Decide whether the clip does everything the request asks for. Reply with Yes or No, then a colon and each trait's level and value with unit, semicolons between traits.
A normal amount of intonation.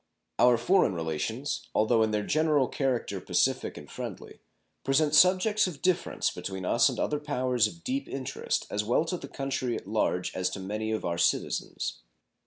No: wide, 6.3 semitones